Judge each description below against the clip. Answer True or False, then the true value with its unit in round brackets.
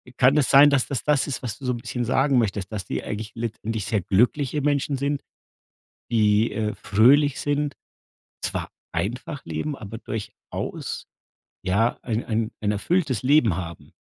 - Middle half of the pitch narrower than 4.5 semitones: False (4.8 semitones)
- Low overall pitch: True (120 Hz)